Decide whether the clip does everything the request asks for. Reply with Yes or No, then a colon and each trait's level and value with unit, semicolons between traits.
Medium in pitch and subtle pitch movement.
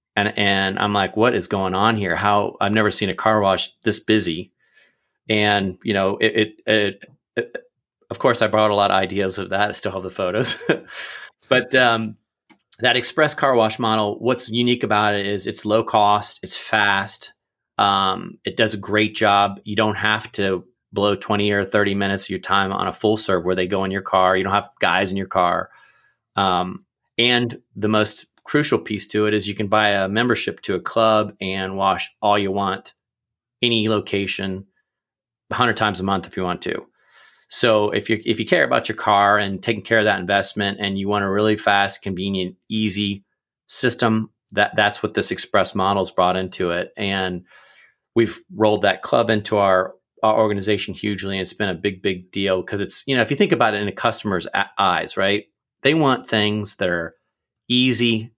No: low, 105 Hz; narrow, 2.0 semitones